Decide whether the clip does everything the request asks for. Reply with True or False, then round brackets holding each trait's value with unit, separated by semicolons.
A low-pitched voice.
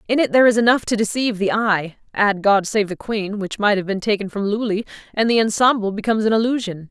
False (210 Hz)